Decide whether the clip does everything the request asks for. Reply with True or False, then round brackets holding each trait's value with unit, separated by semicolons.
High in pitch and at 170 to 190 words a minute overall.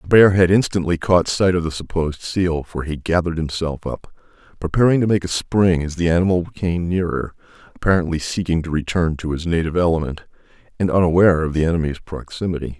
False (85 Hz; 185 wpm)